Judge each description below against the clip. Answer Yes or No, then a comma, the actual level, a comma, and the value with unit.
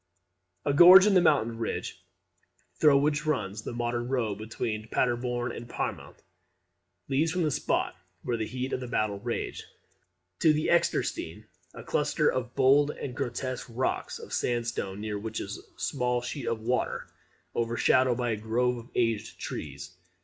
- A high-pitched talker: No, low, 120 Hz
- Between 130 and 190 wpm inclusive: Yes, average, 160 wpm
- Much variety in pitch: No, average, 3.4 semitones